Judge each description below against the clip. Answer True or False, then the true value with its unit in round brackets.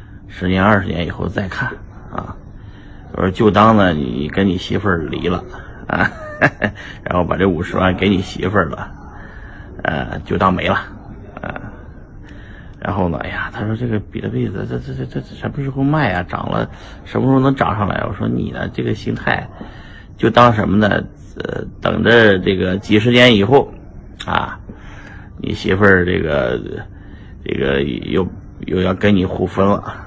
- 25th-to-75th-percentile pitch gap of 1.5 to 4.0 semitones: True (2.4 semitones)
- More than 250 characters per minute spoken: False (235 characters per minute)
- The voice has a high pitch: False (100 Hz)